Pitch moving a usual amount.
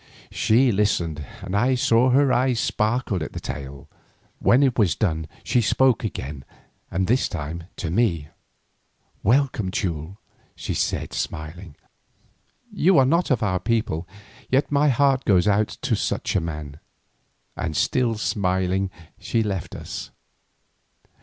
No: wide, 6.9 semitones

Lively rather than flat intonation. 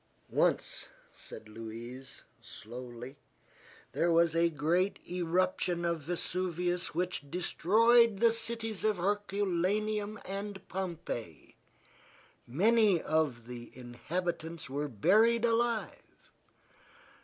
Yes: wide, 5.7 semitones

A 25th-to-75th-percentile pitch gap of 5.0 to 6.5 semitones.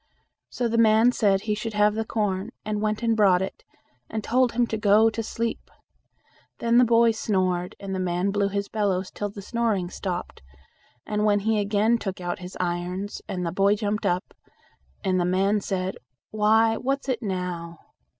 No: average, 3.0 semitones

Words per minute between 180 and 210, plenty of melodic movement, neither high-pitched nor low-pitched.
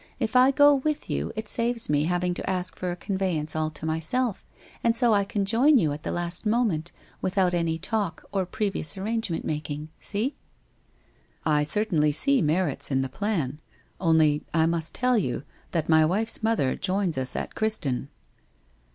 Yes: average, 185 wpm; wide, 5.9 semitones; medium, 180 Hz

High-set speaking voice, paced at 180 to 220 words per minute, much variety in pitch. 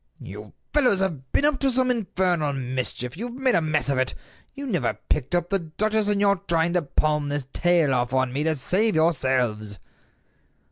No: medium, 165 Hz; average, 195 wpm; wide, 7.2 semitones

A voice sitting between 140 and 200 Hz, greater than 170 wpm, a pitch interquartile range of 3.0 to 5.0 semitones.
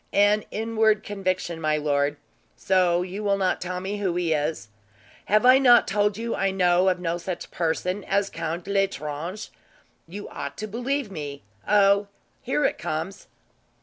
No: high, 190 Hz; average, 160 wpm; average, 3.4 semitones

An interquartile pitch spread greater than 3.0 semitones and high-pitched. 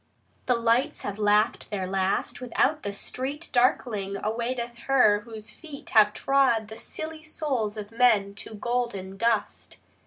Yes: average, 3.5 semitones; high, 230 Hz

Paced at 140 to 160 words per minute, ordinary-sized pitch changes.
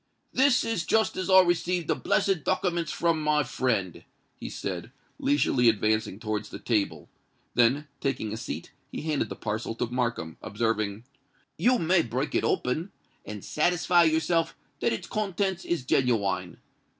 No: average, 150 wpm; wide, 8.0 semitones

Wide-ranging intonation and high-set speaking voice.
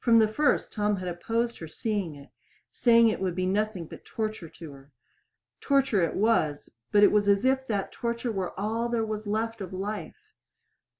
No: average, 3.7 semitones; high, 210 Hz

